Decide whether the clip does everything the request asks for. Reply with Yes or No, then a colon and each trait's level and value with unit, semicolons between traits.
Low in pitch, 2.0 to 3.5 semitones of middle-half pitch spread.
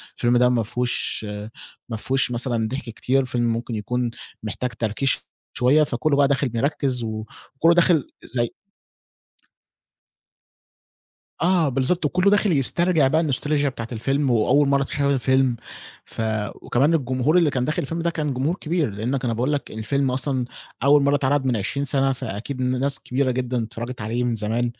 Yes: low, 130 Hz; average, 3.1 semitones